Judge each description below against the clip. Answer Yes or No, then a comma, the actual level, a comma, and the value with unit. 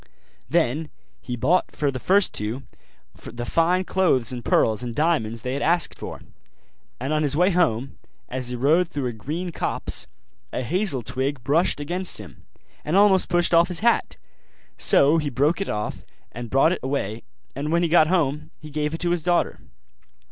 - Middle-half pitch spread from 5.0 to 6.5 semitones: Yes, wide, 5.4 semitones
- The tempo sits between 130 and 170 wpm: No, average, 185 wpm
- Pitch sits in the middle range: Yes, medium, 150 Hz